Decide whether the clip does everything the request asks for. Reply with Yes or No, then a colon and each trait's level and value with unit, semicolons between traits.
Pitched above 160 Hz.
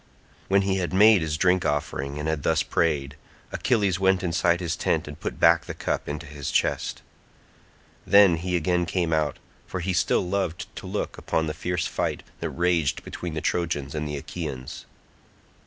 No: very low, 85 Hz